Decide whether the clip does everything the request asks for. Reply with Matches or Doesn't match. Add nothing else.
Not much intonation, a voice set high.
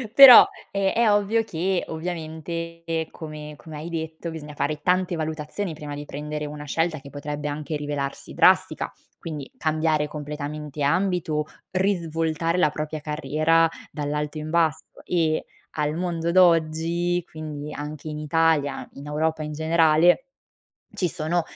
Doesn't match